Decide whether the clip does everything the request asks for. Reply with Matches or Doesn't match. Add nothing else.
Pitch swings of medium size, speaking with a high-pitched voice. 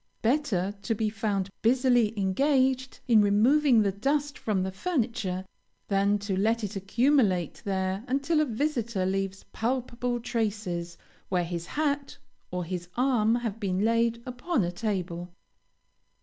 Matches